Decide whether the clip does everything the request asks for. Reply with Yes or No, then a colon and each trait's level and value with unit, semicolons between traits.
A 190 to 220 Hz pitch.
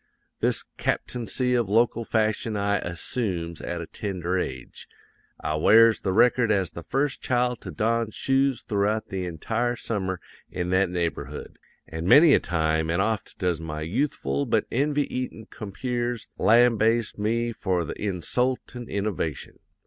No: low, 105 Hz